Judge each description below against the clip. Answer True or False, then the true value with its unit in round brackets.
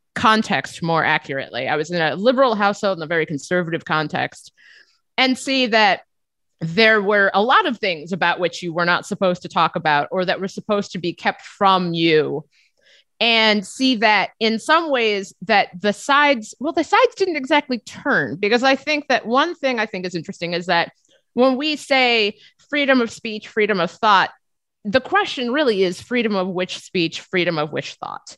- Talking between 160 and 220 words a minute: True (190 wpm)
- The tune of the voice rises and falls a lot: True (6.5 semitones)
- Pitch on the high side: True (205 Hz)